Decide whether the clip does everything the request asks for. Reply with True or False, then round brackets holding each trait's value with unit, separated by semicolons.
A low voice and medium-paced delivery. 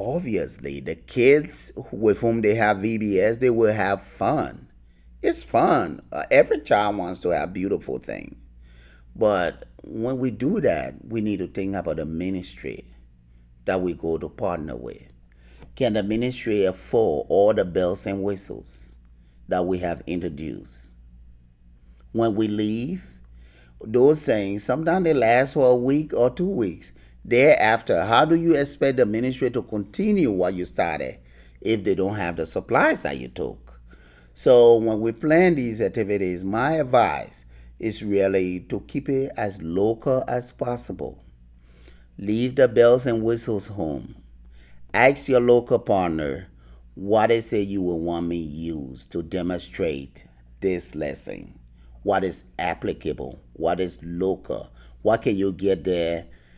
True (90 Hz; 145 wpm)